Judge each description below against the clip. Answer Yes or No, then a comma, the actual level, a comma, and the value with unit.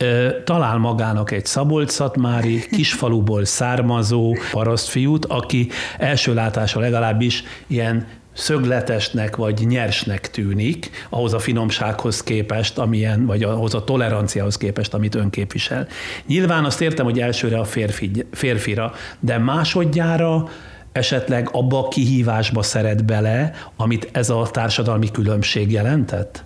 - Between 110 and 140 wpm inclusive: Yes, average, 115 wpm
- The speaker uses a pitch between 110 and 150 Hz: Yes, low, 115 Hz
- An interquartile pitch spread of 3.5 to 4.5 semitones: No, average, 2.8 semitones